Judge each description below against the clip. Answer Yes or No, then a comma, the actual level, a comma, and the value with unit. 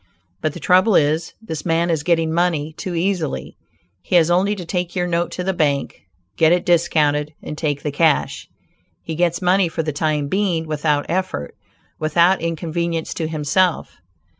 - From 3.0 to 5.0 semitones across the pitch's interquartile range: No, narrow, 2.5 semitones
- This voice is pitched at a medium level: Yes, medium, 165 Hz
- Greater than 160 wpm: Yes, average, 170 wpm